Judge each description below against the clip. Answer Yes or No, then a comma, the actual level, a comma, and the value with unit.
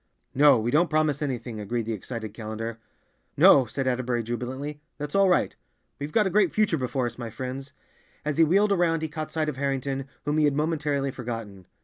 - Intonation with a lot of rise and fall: No, average, 4.3 semitones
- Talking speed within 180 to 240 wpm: Yes, average, 200 wpm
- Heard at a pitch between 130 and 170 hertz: Yes, low, 135 Hz